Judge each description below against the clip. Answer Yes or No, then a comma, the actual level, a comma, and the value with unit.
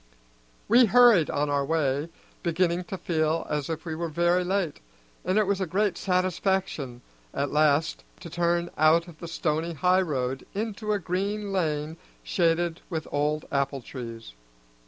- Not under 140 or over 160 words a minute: Yes, average, 155 wpm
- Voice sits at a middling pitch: Yes, medium, 170 Hz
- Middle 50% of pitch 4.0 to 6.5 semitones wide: No, average, 3.6 semitones